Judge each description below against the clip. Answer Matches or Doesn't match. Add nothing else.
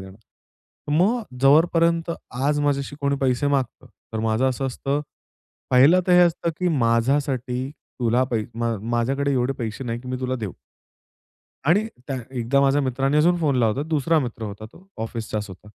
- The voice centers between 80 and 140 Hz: Matches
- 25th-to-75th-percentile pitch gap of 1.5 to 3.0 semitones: Doesn't match